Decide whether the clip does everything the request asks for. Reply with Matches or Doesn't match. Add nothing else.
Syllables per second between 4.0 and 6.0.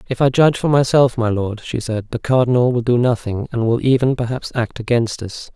Matches